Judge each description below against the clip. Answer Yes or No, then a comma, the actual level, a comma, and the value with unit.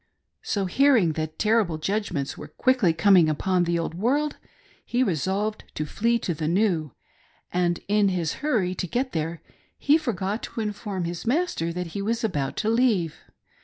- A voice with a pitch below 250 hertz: Yes, high, 190 Hz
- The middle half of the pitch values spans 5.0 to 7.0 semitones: Yes, average, 5.3 semitones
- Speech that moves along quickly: No, average, 170 wpm